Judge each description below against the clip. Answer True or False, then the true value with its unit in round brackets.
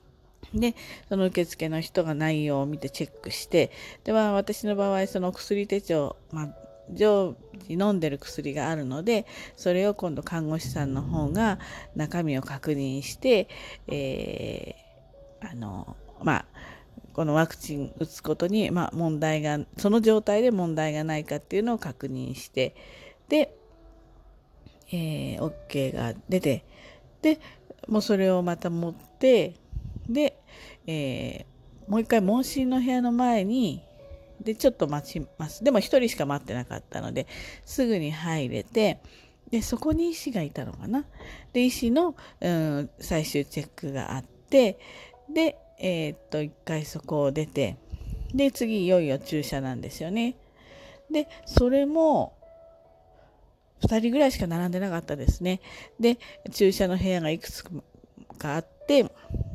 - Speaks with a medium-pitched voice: True (175 Hz)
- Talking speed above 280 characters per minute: False (255 characters per minute)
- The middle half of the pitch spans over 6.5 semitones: True (7.2 semitones)